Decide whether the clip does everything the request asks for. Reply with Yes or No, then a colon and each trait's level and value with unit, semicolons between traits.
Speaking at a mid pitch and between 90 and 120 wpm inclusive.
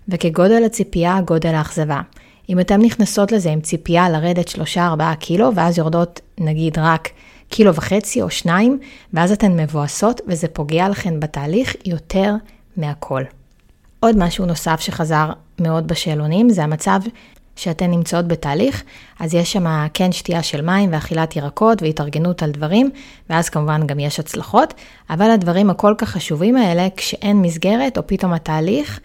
No: medium, 175 Hz; average, 145 wpm